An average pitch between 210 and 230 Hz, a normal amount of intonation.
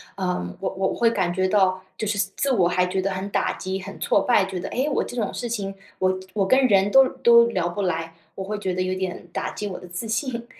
No: high, 195 Hz; average, 3.5 semitones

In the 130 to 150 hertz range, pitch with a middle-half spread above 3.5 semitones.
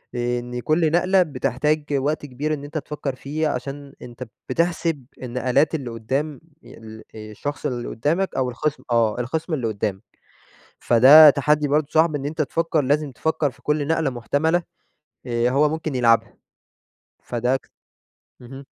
Yes: medium, 140 Hz; average, 3.9 semitones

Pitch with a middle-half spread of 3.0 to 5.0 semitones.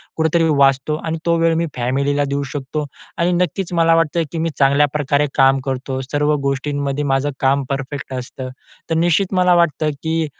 Yes: average, 3.3 semitones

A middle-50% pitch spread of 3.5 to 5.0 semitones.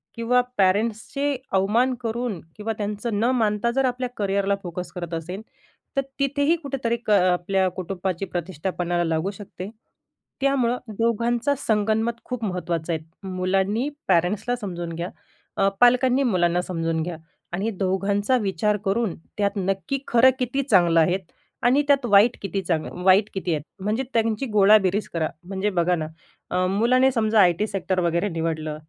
Yes: average, 4.6 semitones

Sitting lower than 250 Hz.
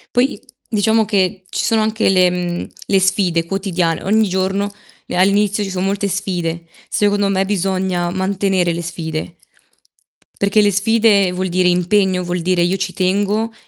Yes: high, 190 Hz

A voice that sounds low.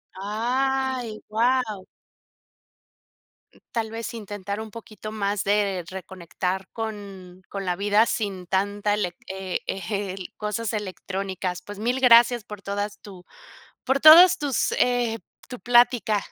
No: high, 210 Hz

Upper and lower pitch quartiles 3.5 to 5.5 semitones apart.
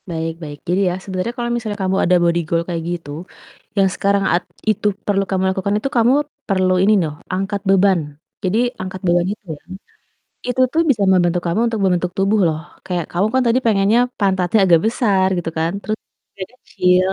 No: average, 2.9 semitones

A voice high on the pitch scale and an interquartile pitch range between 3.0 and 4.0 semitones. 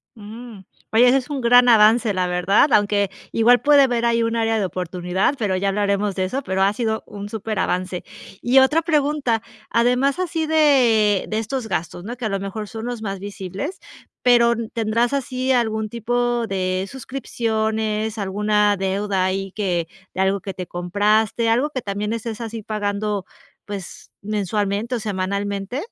Yes: high, 215 Hz; average, 3.5 semitones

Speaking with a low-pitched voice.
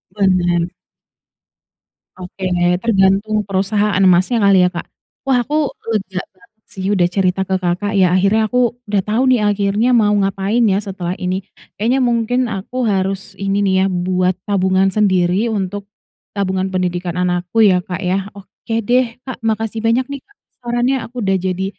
No: high, 195 Hz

